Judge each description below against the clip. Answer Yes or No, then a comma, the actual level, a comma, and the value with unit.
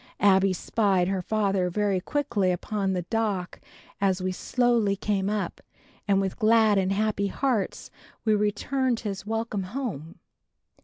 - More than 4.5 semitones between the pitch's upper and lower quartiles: No, narrow, 2.5 semitones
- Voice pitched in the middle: No, high, 200 Hz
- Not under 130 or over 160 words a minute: Yes, average, 140 wpm